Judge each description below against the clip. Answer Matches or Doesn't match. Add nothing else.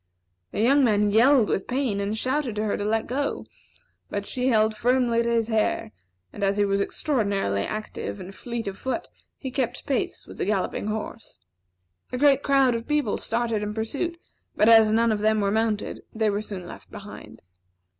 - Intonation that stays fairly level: Doesn't match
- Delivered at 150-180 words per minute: Doesn't match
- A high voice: Matches